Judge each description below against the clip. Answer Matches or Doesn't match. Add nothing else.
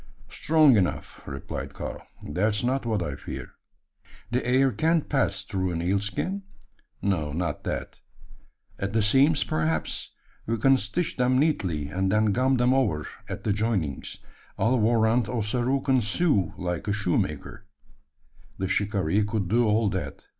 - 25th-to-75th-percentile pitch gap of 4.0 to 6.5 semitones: Matches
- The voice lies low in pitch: Matches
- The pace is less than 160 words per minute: Matches